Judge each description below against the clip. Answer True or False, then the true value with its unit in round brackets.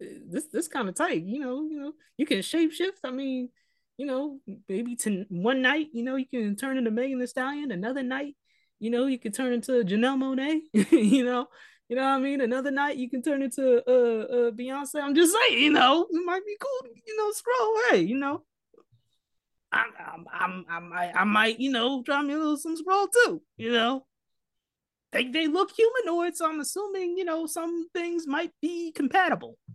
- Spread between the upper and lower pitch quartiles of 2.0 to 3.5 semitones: False (5.2 semitones)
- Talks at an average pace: False (210 wpm)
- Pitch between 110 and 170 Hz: False (275 Hz)